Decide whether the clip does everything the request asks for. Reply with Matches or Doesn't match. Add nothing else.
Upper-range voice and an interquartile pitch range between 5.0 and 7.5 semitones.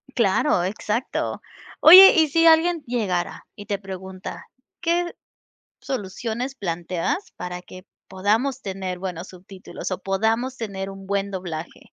Matches